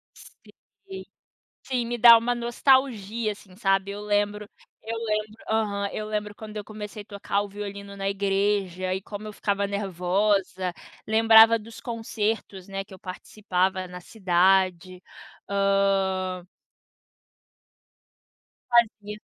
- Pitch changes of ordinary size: No, narrow, 2.0 semitones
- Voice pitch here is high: Yes, high, 205 Hz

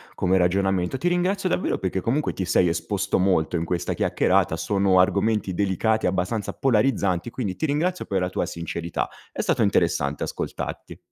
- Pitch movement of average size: Yes, average, 4.2 semitones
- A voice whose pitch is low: Yes, very low, 95 Hz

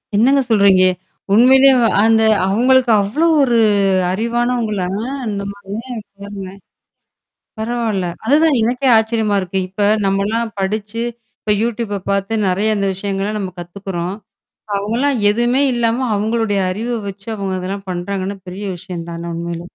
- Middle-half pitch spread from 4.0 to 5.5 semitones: No, average, 3.2 semitones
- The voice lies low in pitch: No, high, 205 Hz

